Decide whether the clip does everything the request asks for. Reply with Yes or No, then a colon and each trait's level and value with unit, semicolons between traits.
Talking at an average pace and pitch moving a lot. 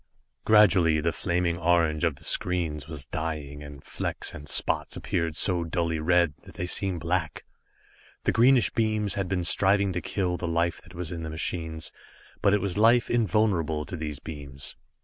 No: average, 175 wpm; average, 3.3 semitones